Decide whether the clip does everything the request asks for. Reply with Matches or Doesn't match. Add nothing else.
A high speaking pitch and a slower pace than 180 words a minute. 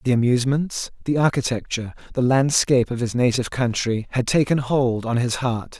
Doesn't match